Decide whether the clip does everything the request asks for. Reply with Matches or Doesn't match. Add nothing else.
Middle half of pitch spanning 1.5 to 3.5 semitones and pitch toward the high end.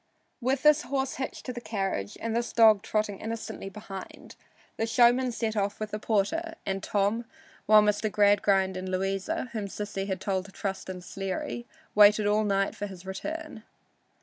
Matches